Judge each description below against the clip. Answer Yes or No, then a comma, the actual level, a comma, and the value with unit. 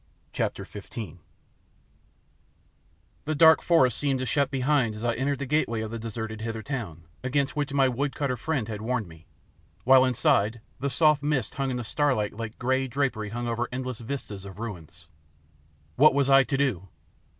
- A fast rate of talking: No, average, 170 wpm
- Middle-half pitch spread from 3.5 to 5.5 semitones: Yes, average, 4.0 semitones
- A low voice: Yes, low, 125 Hz